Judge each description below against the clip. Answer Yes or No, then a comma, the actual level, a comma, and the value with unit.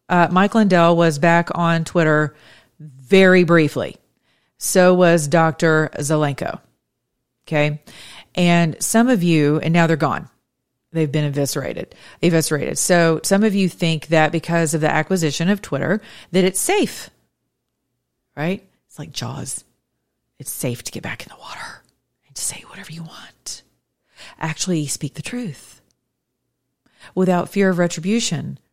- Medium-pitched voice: Yes, medium, 165 Hz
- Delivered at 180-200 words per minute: No, average, 140 wpm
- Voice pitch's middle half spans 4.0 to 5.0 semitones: No, average, 2.9 semitones